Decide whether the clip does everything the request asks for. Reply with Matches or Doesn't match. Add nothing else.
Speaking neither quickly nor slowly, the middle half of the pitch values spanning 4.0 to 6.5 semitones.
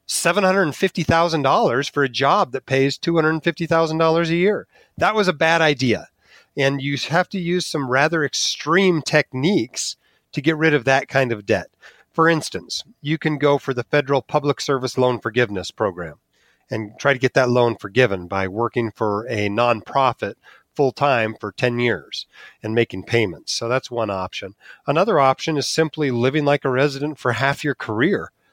Matches